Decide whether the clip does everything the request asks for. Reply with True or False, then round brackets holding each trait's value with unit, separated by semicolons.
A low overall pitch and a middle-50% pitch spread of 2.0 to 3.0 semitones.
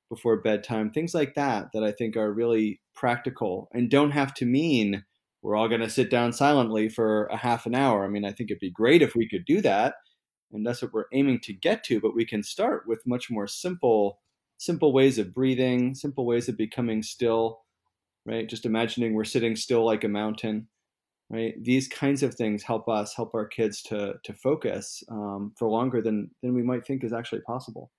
True (115 Hz; 2.5 semitones)